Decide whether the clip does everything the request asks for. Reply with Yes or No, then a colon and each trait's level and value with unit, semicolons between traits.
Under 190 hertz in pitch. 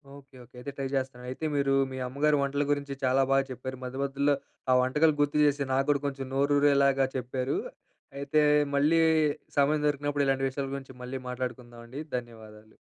Yes: low, 135 Hz